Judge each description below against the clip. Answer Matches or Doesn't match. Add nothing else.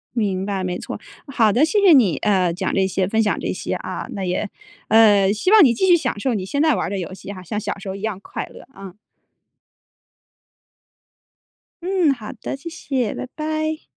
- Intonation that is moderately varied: Doesn't match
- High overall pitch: Matches